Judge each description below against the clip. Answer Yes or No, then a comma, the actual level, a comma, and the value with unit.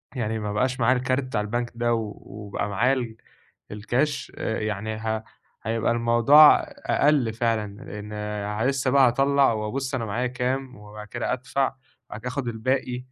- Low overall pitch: Yes, low, 115 Hz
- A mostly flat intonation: No, average, 3.1 semitones